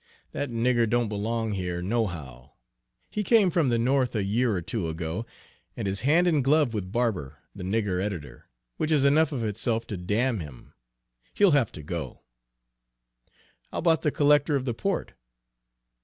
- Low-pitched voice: Yes, low, 115 Hz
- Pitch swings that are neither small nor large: No, wide, 6.6 semitones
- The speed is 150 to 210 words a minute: Yes, average, 170 wpm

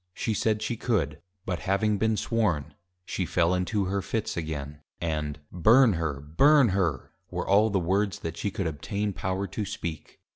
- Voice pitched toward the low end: Yes, very low, 95 Hz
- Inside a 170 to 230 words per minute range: Yes, average, 175 wpm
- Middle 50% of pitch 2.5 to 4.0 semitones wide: No, average, 4.5 semitones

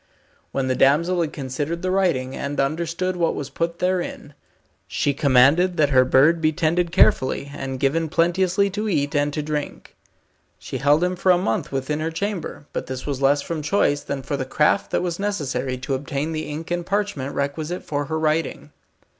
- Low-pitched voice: No, medium, 155 Hz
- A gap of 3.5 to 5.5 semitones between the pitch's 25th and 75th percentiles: Yes, average, 3.9 semitones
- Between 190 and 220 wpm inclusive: Yes, average, 195 wpm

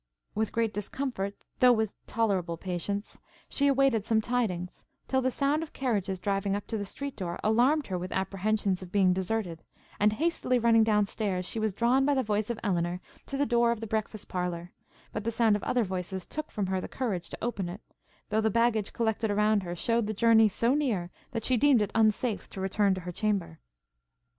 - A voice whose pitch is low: No, high, 215 Hz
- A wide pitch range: No, average, 3.6 semitones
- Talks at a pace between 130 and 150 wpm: No, fast, 205 wpm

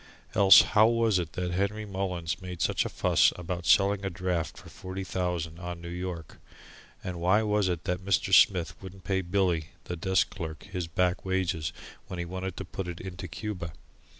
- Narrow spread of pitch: Yes, narrow, 1.9 semitones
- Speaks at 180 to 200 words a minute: Yes, average, 190 wpm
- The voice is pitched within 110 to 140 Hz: No, very low, 90 Hz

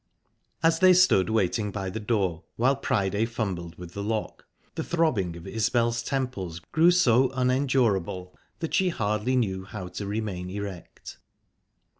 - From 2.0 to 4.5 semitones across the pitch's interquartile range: No, average, 5.2 semitones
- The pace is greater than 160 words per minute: No, average, 145 wpm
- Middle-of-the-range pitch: No, low, 110 Hz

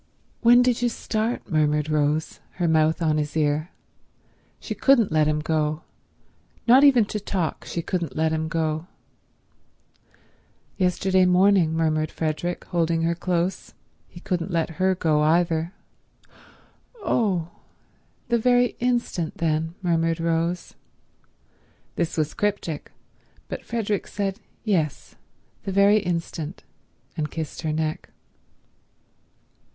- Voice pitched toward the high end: No, medium, 170 Hz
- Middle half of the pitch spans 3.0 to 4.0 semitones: Yes, average, 3.7 semitones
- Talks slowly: Yes, slow, 115 wpm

